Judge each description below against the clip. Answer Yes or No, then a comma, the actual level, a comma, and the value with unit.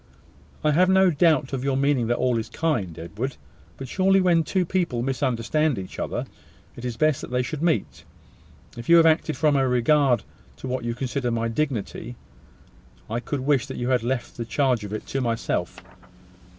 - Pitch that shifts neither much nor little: Yes, average, 4.3 semitones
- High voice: No, low, 130 Hz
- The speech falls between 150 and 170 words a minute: No, average, 190 wpm